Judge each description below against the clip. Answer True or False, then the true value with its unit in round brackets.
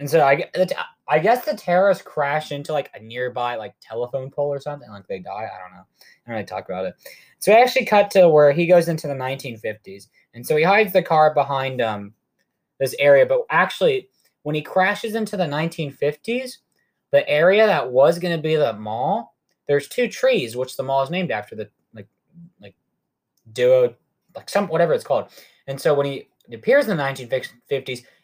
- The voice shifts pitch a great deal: True (6.9 semitones)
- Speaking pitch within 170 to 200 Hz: False (155 Hz)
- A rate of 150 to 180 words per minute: False (200 wpm)